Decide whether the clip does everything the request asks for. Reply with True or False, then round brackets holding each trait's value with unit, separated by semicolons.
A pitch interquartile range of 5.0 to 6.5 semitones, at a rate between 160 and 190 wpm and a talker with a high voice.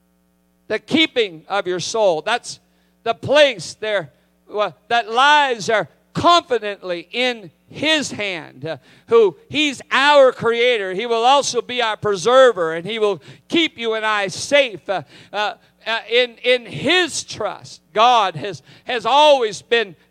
False (5.6 semitones; 140 wpm; 230 Hz)